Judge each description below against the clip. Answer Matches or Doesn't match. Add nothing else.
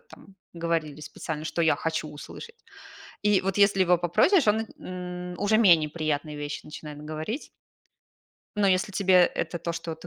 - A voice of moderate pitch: Matches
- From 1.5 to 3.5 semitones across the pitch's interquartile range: Doesn't match